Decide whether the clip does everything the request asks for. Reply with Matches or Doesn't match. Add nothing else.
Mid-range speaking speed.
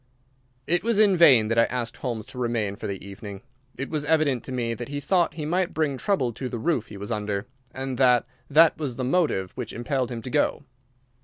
Doesn't match